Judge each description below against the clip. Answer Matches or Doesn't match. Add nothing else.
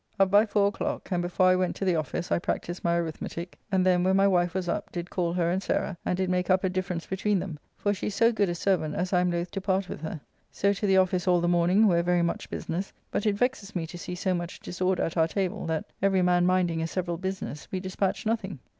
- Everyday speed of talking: Doesn't match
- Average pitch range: Doesn't match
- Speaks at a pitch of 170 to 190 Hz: Matches